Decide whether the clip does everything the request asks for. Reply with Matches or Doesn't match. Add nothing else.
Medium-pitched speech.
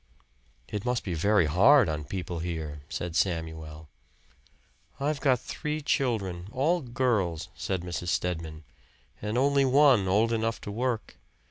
Doesn't match